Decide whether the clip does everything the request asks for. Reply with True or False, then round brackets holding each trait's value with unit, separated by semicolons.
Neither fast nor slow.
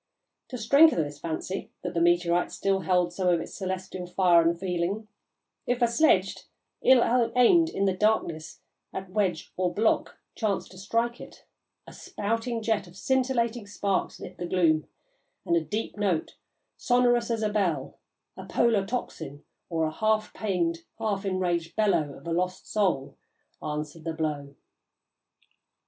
True (155 wpm)